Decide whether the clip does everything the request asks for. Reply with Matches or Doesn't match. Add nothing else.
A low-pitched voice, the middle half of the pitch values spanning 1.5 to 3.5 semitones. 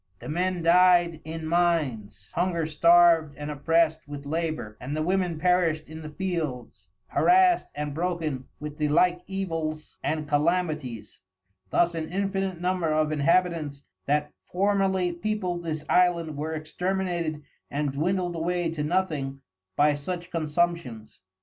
Doesn't match